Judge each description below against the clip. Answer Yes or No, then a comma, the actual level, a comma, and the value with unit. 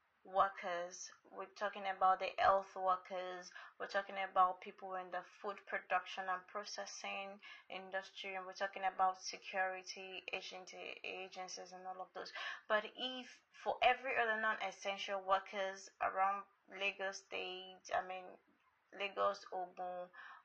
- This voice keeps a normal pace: No, slow, 130 wpm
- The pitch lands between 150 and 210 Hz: Yes, high, 190 Hz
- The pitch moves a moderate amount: No, narrow, 1.2 semitones